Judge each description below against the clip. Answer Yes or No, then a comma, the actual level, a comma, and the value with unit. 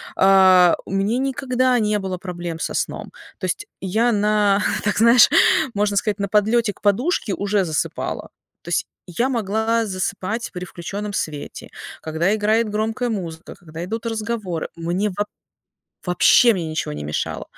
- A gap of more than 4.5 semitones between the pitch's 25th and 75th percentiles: No, average, 3.7 semitones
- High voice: Yes, high, 205 Hz